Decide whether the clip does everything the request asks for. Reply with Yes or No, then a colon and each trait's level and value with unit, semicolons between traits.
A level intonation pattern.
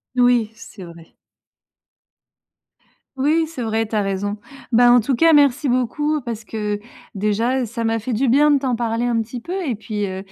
No: average, 3.6 semitones